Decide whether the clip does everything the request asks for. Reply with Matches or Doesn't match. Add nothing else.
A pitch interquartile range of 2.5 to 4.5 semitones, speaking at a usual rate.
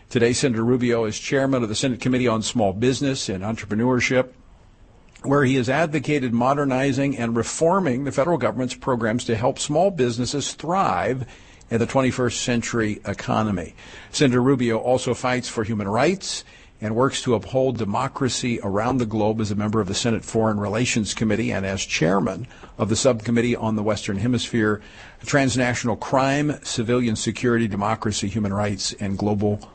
Matches